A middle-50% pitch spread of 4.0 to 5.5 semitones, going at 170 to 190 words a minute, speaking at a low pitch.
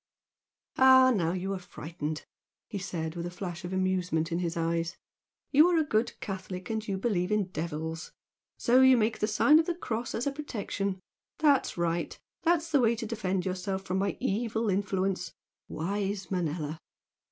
No: average, 4.6 semitones; average, 175 wpm; high, 195 Hz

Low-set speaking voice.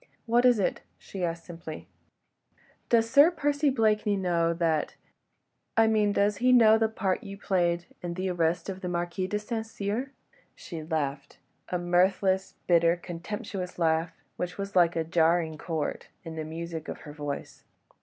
No: medium, 180 Hz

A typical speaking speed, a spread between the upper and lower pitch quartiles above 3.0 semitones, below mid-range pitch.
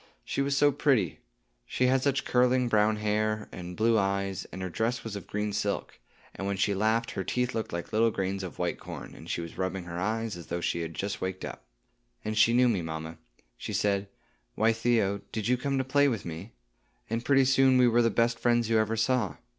No: fast, 225 wpm; average, 3.9 semitones; low, 110 Hz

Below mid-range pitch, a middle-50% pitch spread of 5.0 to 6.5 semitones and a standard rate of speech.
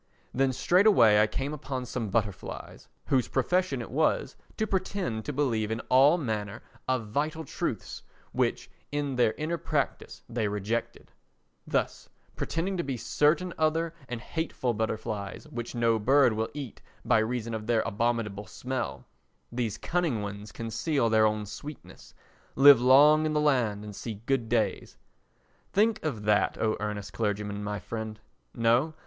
Yes: low, 120 Hz; average, 5.3 semitones; average, 150 wpm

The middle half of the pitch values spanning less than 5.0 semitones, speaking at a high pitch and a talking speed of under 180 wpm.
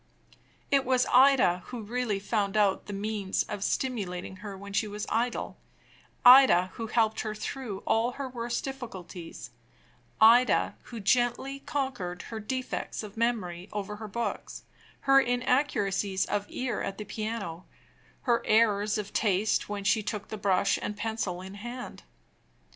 Yes: average, 3.6 semitones; high, 215 Hz; average, 150 wpm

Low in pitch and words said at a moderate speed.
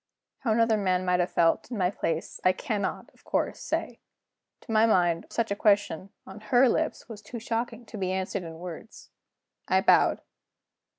No: high, 200 Hz; average, 180 wpm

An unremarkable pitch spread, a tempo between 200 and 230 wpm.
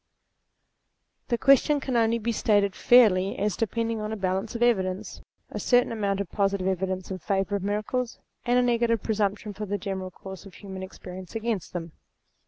No: average, 3.3 semitones; average, 180 wpm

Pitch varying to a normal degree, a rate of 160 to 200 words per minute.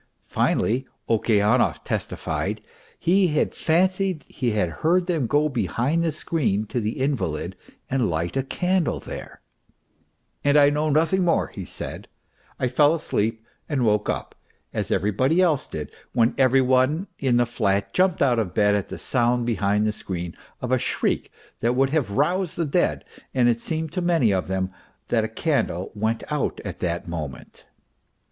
No: wide, 6.5 semitones; average, 170 wpm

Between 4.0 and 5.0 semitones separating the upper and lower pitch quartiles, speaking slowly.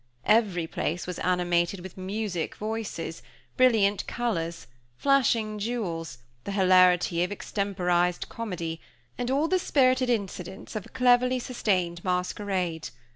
Yes: average, 4.5 semitones; slow, 115 wpm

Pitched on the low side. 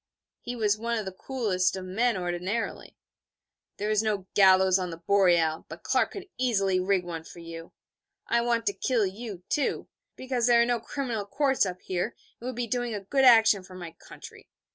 No: high, 205 Hz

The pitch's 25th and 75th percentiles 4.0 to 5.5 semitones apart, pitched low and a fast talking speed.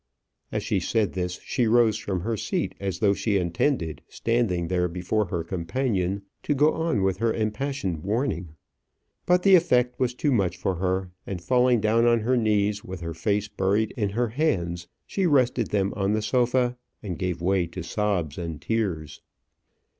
No: average, 5.0 semitones; low, 105 Hz; average, 175 wpm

